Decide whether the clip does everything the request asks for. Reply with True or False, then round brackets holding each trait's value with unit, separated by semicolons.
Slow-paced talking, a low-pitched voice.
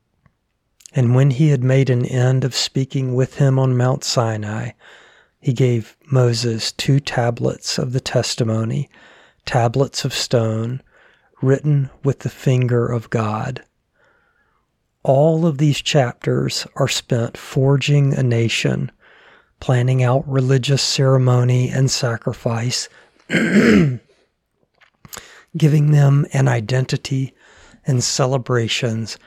True (105 wpm; 130 Hz)